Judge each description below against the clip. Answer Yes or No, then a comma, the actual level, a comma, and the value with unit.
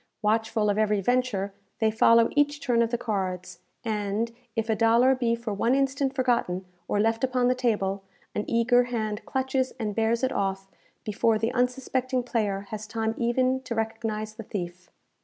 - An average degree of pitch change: Yes, average, 3.0 semitones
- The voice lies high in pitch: Yes, high, 225 Hz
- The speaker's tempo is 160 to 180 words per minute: Yes, average, 175 wpm